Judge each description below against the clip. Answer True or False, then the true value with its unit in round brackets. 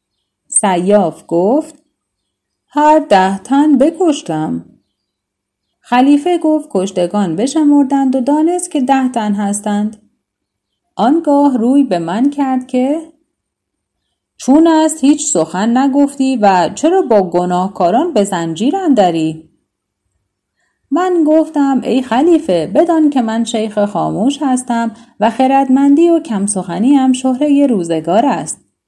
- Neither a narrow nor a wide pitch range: False (7.4 semitones)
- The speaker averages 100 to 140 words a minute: True (110 wpm)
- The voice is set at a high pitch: True (255 Hz)